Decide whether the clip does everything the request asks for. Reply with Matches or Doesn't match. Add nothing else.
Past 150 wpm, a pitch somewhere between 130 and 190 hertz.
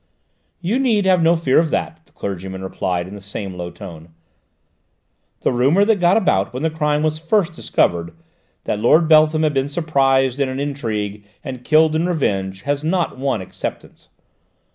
Matches